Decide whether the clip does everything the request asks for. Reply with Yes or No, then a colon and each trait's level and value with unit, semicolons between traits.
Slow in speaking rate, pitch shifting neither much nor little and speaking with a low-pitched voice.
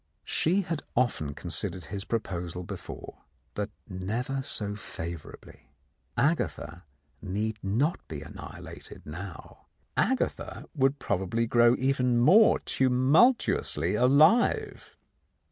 No: slow, 95 wpm; wide, 6.6 semitones; low, 115 Hz